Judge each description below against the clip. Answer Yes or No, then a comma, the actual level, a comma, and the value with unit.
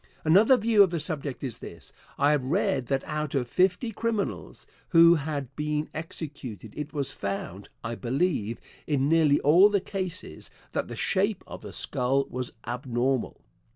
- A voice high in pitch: No, medium, 150 Hz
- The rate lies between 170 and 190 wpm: No, average, 160 wpm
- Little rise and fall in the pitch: No, average, 5.2 semitones